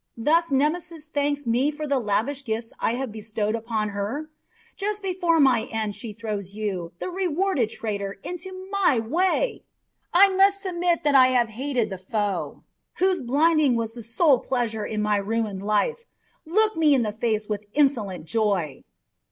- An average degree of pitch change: No, wide, 7.3 semitones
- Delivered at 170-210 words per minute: No, average, 160 wpm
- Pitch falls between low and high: No, very high, 250 Hz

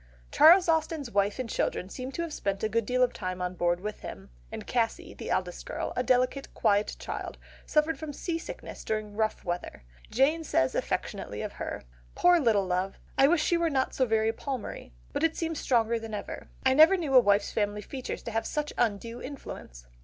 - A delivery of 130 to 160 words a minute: No, average, 200 wpm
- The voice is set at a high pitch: Yes, high, 235 Hz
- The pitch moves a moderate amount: No, wide, 6.4 semitones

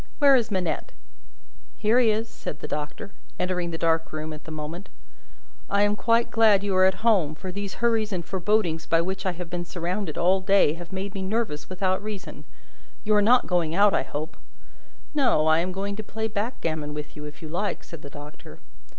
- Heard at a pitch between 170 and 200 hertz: Yes, medium, 185 Hz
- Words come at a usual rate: No, fast, 210 wpm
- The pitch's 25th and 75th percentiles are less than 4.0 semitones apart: No, average, 4.3 semitones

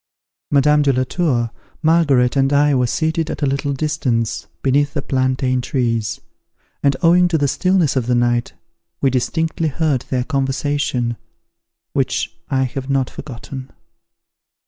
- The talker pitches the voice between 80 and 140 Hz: Yes, low, 135 Hz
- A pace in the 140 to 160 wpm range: Yes, average, 145 wpm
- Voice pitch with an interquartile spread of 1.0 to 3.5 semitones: Yes, average, 2.7 semitones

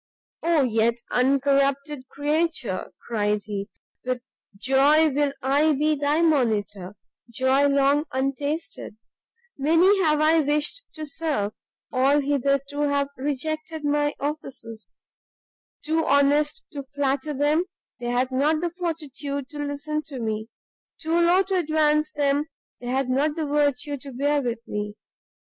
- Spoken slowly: Yes, slow, 130 wpm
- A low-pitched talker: No, very high, 285 Hz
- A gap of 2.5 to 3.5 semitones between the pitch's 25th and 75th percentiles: Yes, average, 2.8 semitones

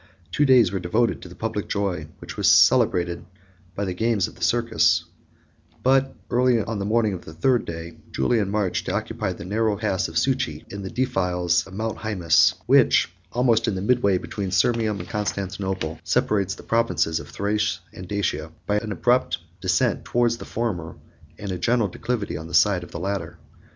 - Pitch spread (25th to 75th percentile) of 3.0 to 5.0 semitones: Yes, average, 4.2 semitones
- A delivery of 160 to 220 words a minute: Yes, average, 185 wpm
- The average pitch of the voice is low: Yes, low, 100 Hz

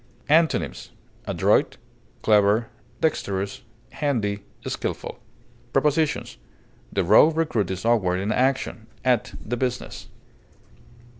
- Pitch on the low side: Yes, low, 115 Hz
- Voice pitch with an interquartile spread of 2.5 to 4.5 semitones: No, average, 5.3 semitones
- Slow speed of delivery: Yes, slow, 90 wpm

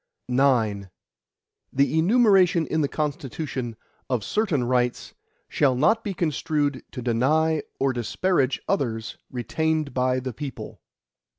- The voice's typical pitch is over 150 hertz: No, medium, 140 Hz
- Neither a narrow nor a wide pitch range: Yes, average, 4.2 semitones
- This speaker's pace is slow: Yes, slow, 115 wpm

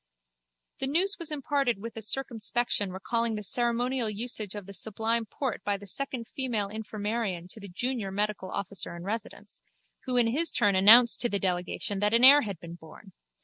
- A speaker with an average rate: Yes, average, 185 wpm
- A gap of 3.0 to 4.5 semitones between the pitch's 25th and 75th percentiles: Yes, average, 3.5 semitones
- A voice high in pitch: Yes, high, 220 Hz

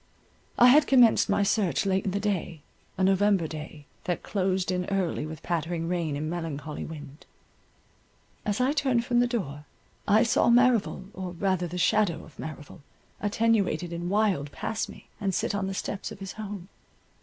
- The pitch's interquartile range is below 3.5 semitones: No, average, 4.1 semitones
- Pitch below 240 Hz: Yes, high, 190 Hz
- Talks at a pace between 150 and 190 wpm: Yes, average, 175 wpm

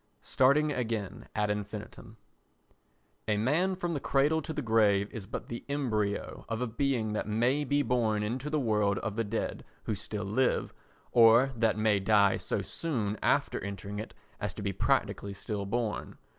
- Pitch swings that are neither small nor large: Yes, average, 4.1 semitones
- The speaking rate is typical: Yes, average, 170 wpm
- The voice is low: Yes, low, 110 Hz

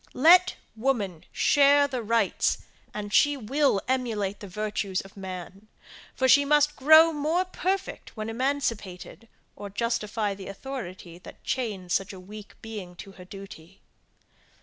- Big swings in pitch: Yes, wide, 6.1 semitones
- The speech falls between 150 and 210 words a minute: No, average, 140 wpm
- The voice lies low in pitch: No, high, 215 Hz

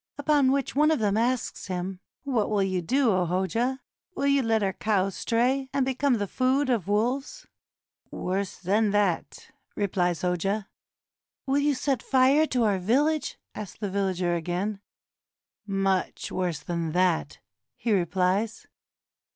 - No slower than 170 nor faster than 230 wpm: No, average, 150 wpm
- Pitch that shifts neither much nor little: No, wide, 5.8 semitones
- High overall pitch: Yes, high, 210 Hz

